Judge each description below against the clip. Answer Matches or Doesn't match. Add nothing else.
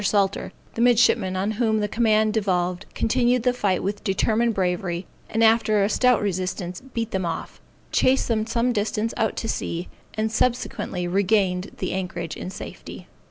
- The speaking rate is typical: Matches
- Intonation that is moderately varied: Matches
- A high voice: Matches